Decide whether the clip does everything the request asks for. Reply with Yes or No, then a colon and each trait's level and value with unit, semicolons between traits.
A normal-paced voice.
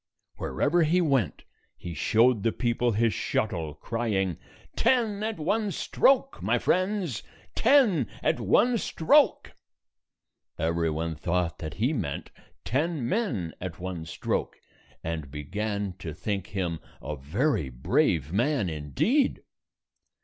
No: slow, 125 wpm